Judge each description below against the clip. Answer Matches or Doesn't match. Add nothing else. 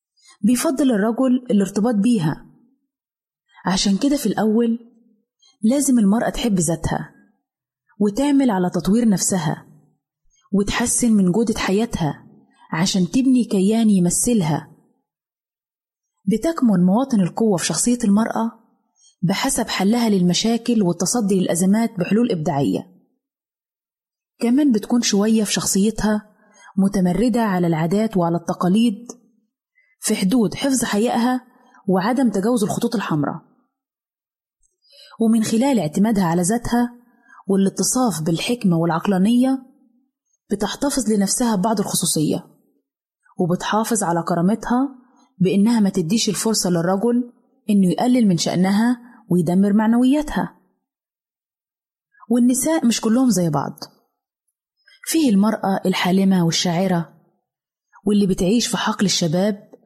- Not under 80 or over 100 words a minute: Matches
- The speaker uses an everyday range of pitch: Matches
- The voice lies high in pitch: Matches